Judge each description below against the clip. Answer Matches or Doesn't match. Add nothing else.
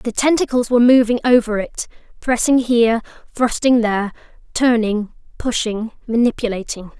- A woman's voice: Matches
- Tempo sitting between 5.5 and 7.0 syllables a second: Doesn't match